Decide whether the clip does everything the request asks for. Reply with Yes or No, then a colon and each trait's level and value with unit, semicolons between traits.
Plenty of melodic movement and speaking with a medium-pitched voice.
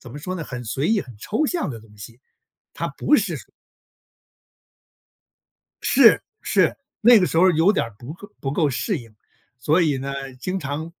Yes: wide, 7.0 semitones; medium, 145 Hz